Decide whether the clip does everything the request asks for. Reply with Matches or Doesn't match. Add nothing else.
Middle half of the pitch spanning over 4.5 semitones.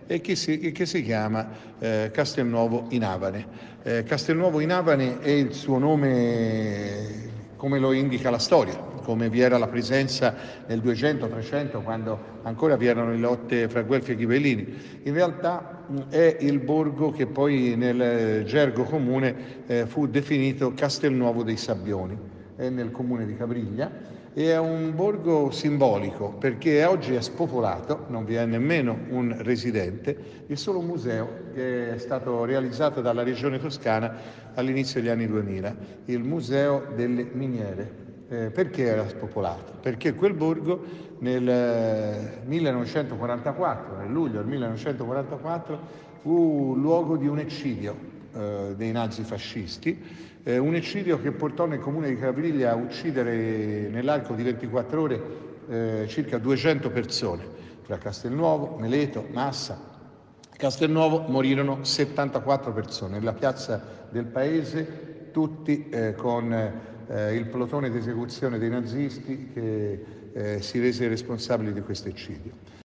Doesn't match